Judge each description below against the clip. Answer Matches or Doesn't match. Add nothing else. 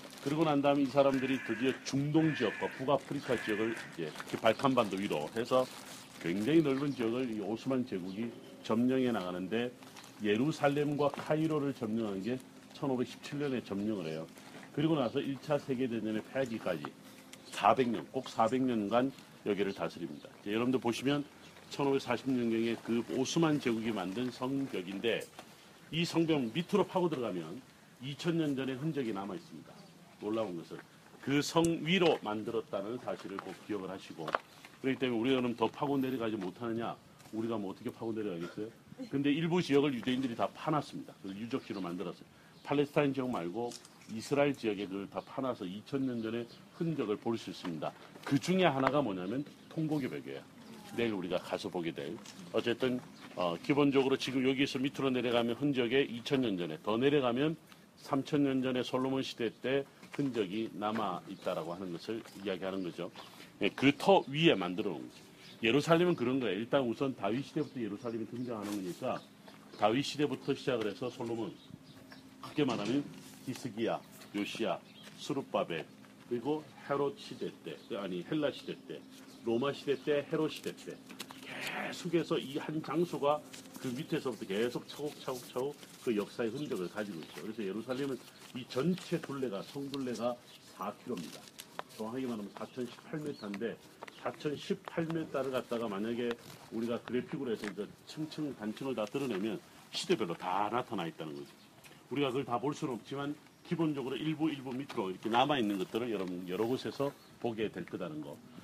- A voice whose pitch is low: Matches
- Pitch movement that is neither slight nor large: Matches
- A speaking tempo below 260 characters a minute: Doesn't match